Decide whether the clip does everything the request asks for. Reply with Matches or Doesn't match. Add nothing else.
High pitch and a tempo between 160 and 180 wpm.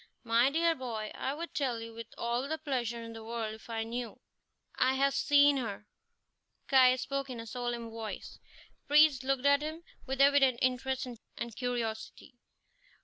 Matches